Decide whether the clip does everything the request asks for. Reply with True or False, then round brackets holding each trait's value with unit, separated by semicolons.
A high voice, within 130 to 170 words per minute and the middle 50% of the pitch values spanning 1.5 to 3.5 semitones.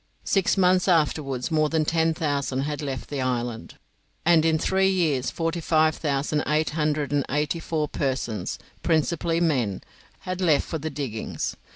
False (155 Hz; 160 wpm; 2.9 semitones)